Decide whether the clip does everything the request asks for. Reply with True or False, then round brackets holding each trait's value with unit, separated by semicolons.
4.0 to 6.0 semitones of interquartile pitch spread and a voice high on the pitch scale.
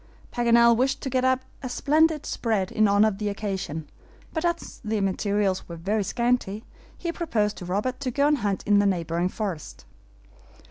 True (4.6 semitones; 215 Hz)